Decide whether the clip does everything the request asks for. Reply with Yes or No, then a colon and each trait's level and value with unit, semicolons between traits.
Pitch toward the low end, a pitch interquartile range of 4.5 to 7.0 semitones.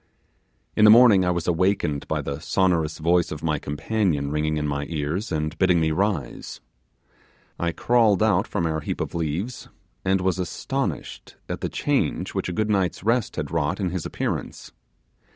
No: very low, 85 Hz; average, 3.8 semitones